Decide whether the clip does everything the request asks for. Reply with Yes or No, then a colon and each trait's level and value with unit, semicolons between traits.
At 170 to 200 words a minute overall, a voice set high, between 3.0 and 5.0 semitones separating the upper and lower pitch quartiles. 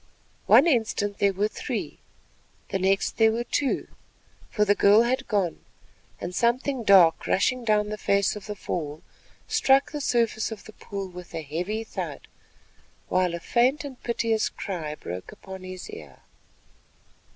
No: average, 150 wpm; high, 205 Hz; average, 4.2 semitones